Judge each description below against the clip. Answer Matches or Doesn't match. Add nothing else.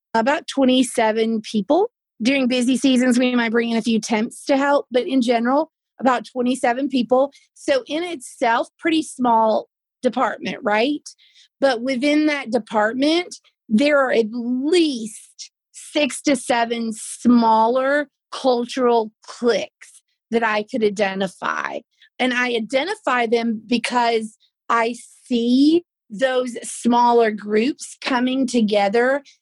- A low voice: Doesn't match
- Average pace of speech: Doesn't match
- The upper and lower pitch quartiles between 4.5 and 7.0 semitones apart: Doesn't match